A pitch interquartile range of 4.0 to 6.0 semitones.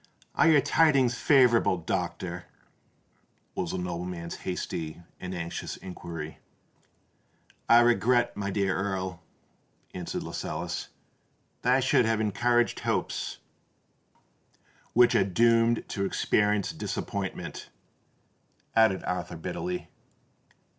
Yes: average, 4.9 semitones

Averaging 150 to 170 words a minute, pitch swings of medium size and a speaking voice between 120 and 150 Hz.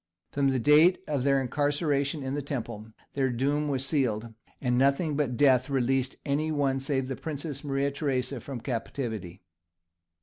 No: average, 160 wpm; narrow, 2.2 semitones; low, 135 Hz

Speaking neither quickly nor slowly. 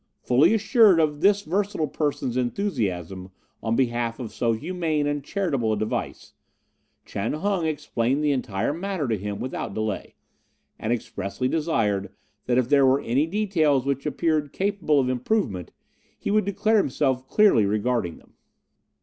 Yes: average, 150 wpm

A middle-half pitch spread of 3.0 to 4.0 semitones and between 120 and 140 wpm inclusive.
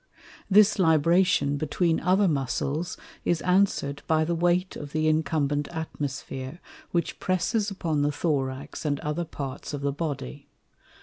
Yes: average, 3.5 semitones; slow, 135 wpm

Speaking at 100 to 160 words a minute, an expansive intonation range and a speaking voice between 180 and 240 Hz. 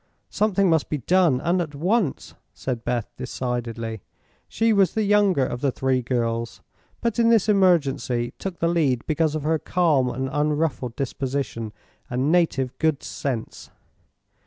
No: average, 150 wpm; wide, 5.9 semitones; medium, 145 Hz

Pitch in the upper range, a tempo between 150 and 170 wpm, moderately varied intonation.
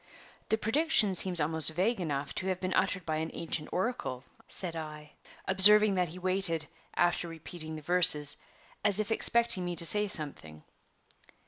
No: medium, 175 Hz; average, 160 wpm; average, 3.7 semitones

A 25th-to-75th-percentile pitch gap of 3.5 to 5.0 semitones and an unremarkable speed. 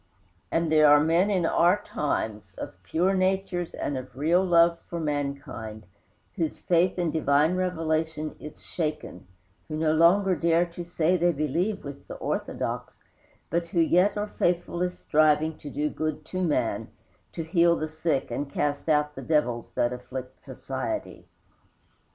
No: average, 2.9 semitones; average, 155 wpm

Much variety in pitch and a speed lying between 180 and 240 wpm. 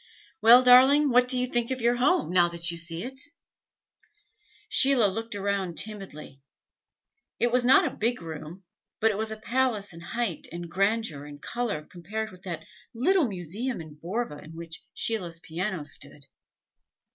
No: wide, 6.3 semitones; average, 165 wpm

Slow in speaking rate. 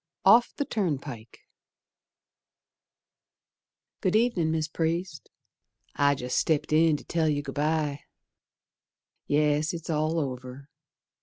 Yes: slow, 105 wpm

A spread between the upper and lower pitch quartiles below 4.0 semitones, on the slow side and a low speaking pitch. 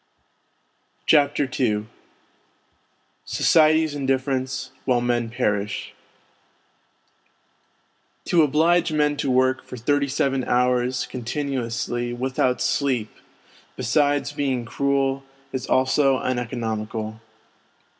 Yes: average, 2.7 semitones; slow, 85 wpm; low, 130 Hz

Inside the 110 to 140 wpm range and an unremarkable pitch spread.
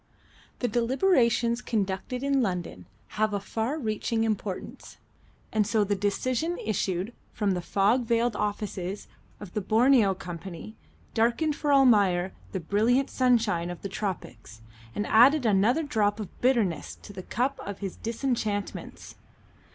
Yes: slow, 135 wpm; average, 3.8 semitones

